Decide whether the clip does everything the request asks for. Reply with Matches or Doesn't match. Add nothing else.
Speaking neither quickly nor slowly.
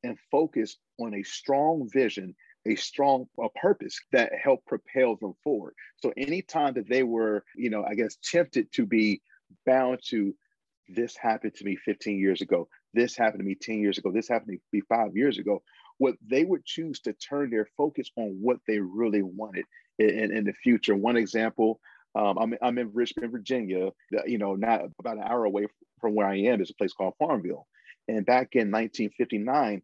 Matches